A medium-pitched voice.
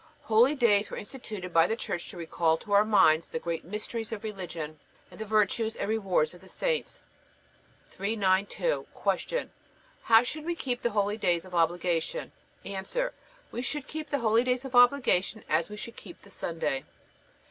No: high, 210 Hz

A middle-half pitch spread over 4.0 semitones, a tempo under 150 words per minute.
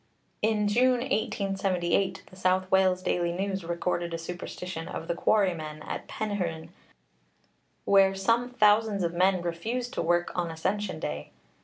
No: average, 3.2 semitones; average, 140 wpm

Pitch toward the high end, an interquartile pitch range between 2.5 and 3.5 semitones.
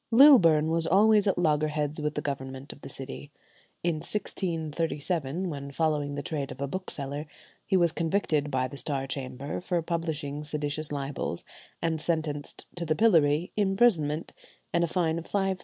No: medium, 155 Hz; average, 3.1 semitones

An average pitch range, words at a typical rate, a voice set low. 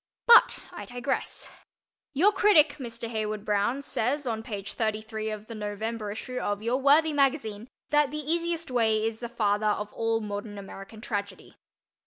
No: average, 4.7 semitones; average, 160 wpm; high, 225 Hz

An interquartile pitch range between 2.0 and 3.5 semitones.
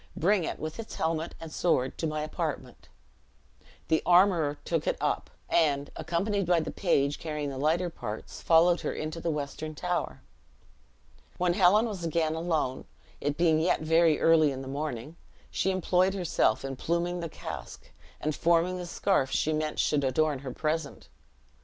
Yes: average, 2.8 semitones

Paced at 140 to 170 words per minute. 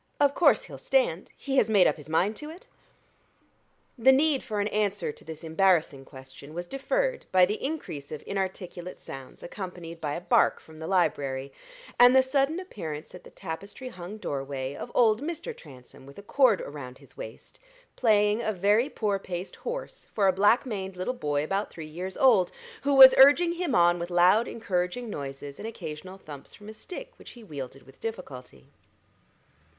No: average, 185 wpm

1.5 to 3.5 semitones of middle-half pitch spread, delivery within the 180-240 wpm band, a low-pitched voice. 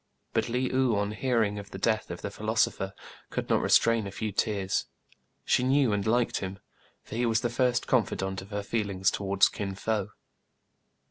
Yes: average, 2.9 semitones; average, 190 wpm; low, 105 Hz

